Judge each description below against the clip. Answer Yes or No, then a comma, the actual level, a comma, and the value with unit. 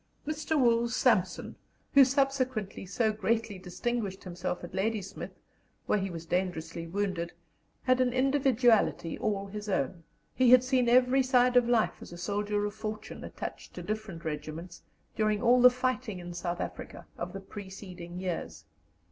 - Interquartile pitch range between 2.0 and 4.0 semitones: No, wide, 5.4 semitones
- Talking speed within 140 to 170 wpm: Yes, average, 155 wpm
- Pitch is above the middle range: Yes, high, 210 Hz